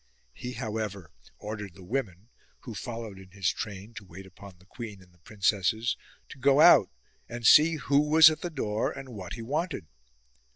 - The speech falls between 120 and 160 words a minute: No, average, 180 wpm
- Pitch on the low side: Yes, low, 110 Hz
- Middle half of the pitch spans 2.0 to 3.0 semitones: No, wide, 5.4 semitones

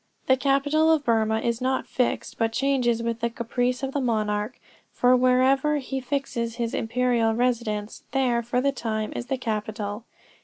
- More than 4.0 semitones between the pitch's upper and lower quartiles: No, average, 2.8 semitones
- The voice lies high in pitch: Yes, high, 245 Hz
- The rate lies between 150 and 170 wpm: Yes, average, 165 wpm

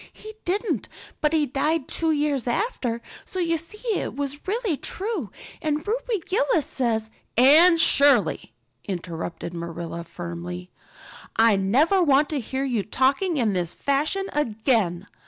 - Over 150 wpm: No, average, 140 wpm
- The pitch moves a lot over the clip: Yes, wide, 7.3 semitones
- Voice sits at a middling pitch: No, very high, 280 Hz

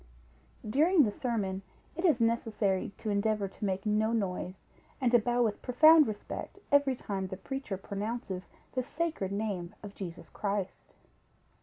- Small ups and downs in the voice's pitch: No, average, 4.1 semitones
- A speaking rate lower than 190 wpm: Yes, average, 150 wpm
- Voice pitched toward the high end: Yes, high, 215 Hz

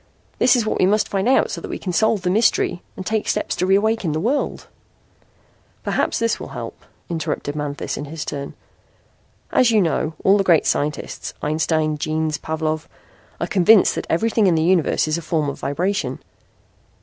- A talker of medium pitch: Yes, medium, 175 Hz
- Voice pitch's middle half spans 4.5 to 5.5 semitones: Yes, average, 5.0 semitones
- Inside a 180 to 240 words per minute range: Yes, average, 185 wpm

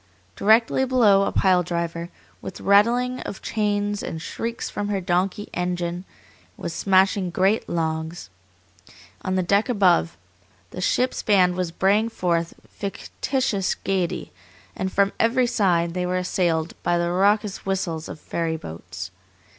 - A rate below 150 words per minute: Yes, average, 140 wpm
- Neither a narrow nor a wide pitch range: Yes, average, 3.1 semitones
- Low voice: No, medium, 185 Hz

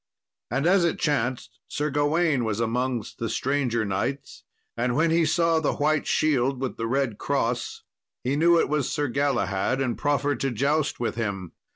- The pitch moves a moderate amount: Yes, average, 3.9 semitones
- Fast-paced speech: No, average, 175 wpm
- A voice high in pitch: No, low, 135 Hz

